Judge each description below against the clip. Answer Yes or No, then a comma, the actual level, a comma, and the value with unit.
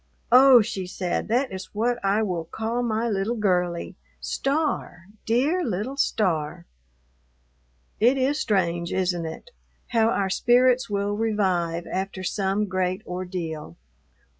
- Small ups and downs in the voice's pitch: No, average, 4.8 semitones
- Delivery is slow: Yes, slow, 125 wpm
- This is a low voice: No, high, 200 Hz